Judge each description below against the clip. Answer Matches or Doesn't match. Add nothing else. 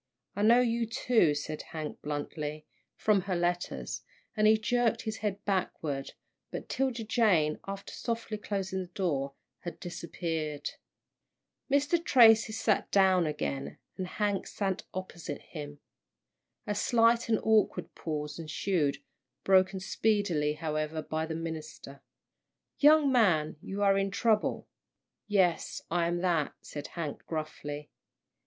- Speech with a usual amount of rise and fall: Doesn't match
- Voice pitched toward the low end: Doesn't match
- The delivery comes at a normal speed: Doesn't match